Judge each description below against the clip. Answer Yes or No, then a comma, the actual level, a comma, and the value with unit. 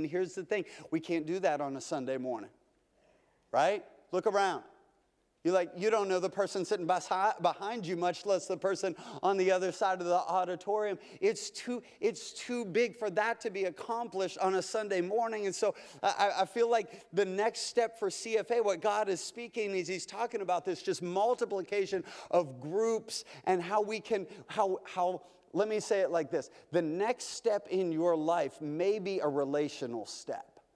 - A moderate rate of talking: Yes, average, 190 wpm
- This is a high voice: Yes, high, 195 Hz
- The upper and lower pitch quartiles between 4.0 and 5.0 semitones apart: No, average, 3.4 semitones